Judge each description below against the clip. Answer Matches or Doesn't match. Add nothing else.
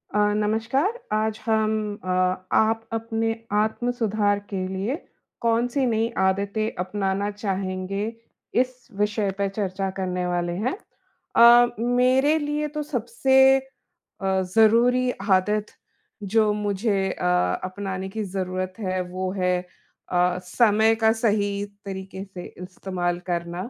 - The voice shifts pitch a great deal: Doesn't match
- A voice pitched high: Matches